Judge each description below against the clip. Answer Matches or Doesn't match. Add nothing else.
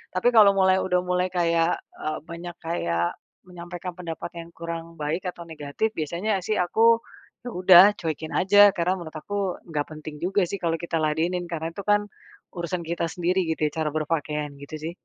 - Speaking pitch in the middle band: Matches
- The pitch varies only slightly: Matches